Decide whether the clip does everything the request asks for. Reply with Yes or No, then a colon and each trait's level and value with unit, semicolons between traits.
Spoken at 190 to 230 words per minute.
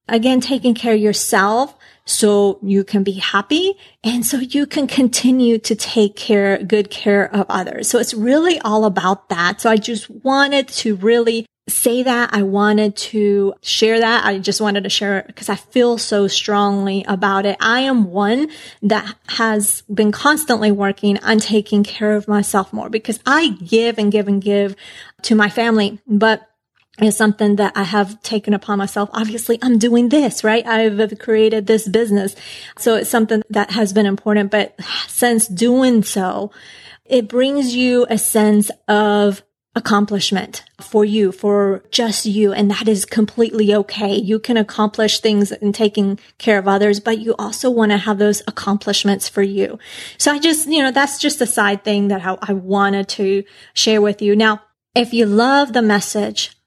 No: average, 175 wpm